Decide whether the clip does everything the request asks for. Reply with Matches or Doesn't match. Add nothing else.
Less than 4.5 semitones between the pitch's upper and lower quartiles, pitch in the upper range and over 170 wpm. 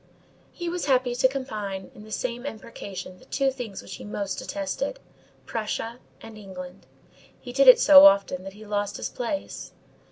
Doesn't match